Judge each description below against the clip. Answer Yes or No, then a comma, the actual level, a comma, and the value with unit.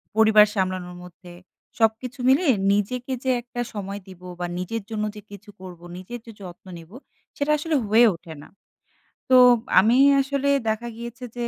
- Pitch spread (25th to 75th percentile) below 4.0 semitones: No, average, 4.6 semitones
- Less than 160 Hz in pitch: No, high, 220 Hz